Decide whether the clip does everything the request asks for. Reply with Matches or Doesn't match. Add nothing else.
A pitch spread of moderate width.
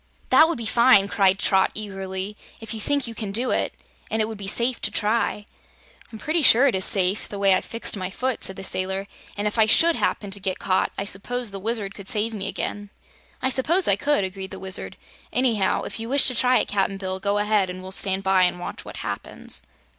Matches